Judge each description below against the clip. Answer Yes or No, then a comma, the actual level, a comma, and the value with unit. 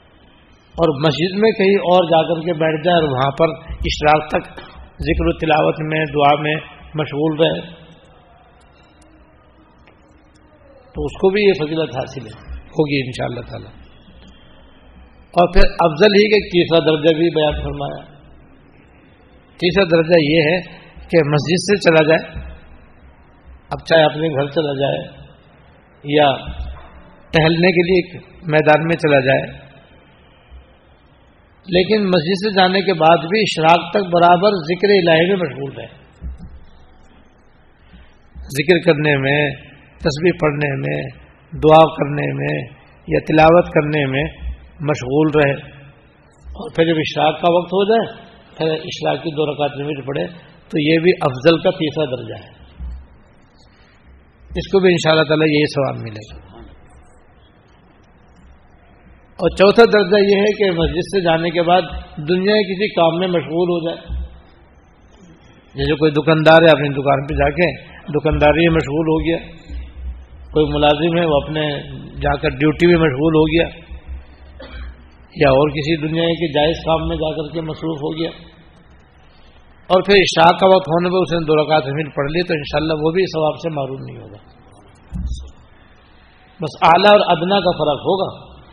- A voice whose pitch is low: No, medium, 155 Hz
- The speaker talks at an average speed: Yes, average, 150 wpm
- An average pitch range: Yes, average, 4.6 semitones